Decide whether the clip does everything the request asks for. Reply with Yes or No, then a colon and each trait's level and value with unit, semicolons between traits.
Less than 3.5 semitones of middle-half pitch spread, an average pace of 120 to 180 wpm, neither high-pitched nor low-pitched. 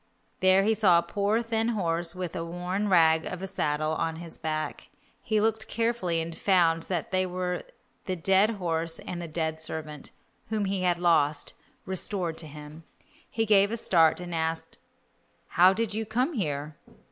No: average, 3.8 semitones; average, 175 wpm; medium, 180 Hz